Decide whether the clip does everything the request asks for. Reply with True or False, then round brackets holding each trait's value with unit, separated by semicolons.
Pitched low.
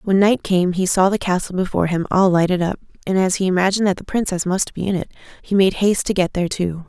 False (185 Hz)